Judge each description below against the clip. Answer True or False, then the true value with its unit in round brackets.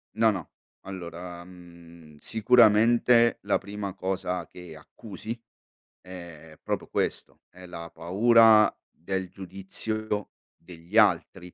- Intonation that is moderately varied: True (3.8 semitones)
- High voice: False (95 Hz)